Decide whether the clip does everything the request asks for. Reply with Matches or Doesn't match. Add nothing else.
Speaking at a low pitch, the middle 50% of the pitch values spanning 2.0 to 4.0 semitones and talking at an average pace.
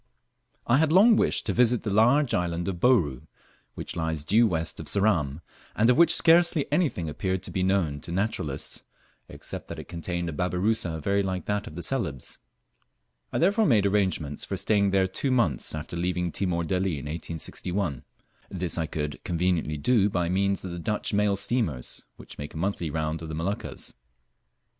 Doesn't match